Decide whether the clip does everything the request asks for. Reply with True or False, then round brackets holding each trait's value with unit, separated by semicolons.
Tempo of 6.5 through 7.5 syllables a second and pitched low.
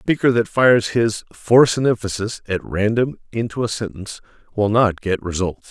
False (5.5 syllables/s; 110 Hz)